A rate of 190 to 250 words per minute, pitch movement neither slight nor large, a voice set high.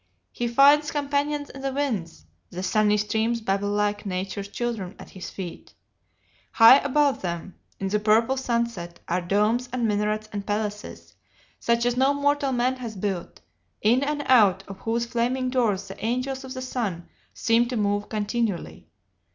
No: average, 160 wpm; average, 4.0 semitones; high, 225 Hz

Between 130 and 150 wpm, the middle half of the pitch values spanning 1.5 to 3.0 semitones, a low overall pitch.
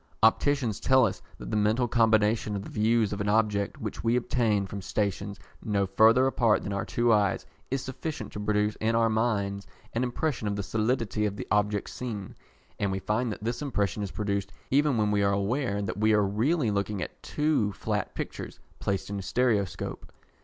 No: average, 195 wpm; average, 2.7 semitones; low, 105 Hz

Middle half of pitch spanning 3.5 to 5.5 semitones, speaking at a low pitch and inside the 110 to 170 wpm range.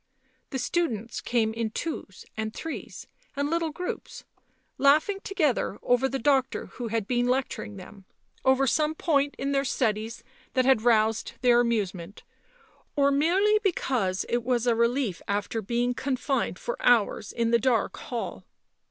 No: average, 4.0 semitones; high, 245 Hz; average, 150 wpm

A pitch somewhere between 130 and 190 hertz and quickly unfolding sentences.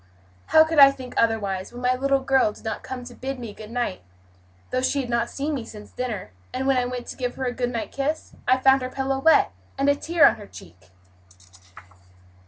No: very high, 255 Hz; fast, 225 wpm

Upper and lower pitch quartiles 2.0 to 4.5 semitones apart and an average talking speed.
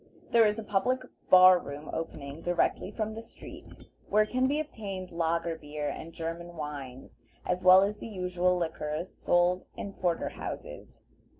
Yes: average, 4.0 semitones; average, 160 wpm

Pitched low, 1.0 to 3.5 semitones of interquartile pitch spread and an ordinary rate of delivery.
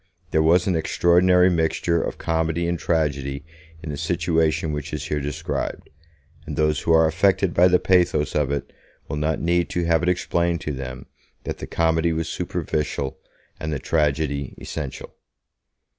Yes: very low, 80 Hz; narrow, 2.4 semitones; average, 165 wpm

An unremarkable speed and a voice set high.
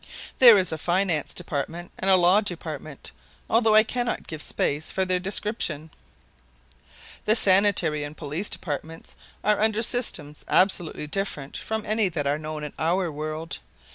No: average, 150 wpm; medium, 175 Hz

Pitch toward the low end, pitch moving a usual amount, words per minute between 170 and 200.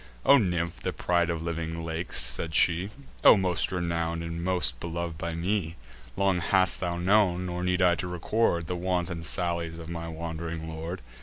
No: very low, 85 Hz; narrow, 1.5 semitones; average, 175 wpm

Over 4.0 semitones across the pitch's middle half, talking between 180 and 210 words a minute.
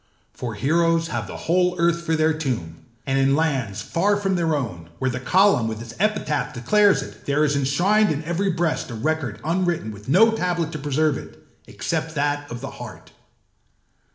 Yes: average, 5.0 semitones; average, 185 wpm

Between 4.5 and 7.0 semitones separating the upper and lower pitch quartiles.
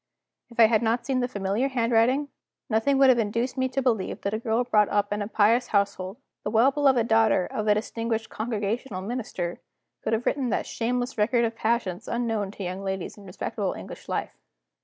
No: average, 3.0 semitones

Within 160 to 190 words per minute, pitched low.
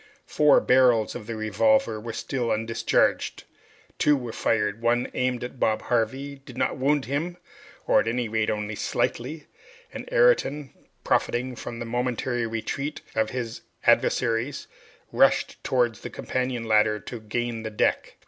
No: average, 150 wpm; low, 120 Hz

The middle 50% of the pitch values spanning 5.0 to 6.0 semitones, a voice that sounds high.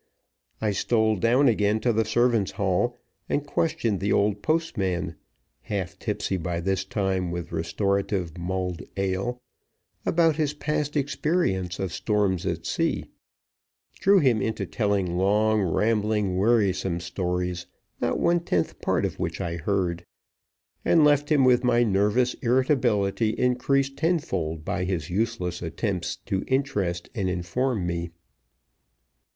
No: average, 5.3 semitones; low, 100 Hz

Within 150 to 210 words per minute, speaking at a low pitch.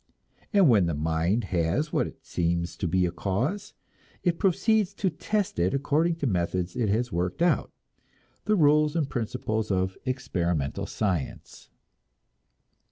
No: average, 140 wpm; low, 110 Hz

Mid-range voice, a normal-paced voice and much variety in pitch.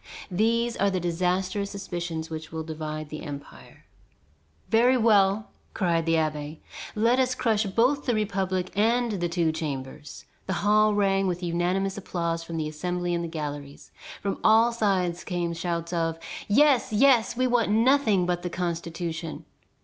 No: medium, 180 Hz; average, 150 wpm; average, 4.4 semitones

